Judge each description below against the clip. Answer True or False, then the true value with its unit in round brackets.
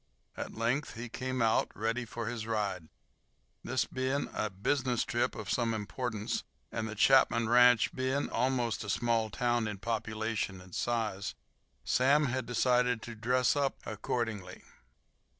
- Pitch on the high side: False (115 Hz)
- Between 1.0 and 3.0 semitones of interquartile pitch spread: True (2.4 semitones)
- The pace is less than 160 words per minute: True (145 wpm)